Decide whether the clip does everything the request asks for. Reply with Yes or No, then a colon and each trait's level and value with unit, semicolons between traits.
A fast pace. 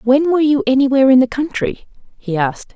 No: average, 195 wpm